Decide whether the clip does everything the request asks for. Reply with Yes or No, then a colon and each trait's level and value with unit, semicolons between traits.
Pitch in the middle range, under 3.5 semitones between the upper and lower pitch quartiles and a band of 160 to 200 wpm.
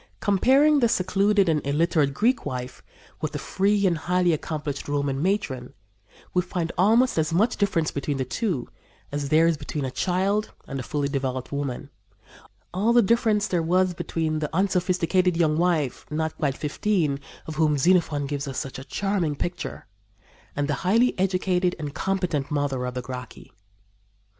No: medium, 165 Hz; average, 4.9 semitones; average, 165 wpm